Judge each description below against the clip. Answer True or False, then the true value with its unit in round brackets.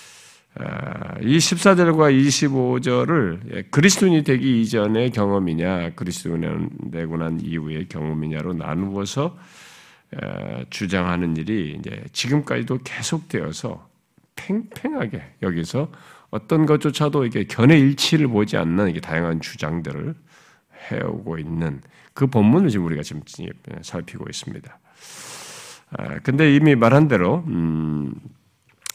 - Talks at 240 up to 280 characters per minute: True (260 characters per minute)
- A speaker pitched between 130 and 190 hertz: False (115 Hz)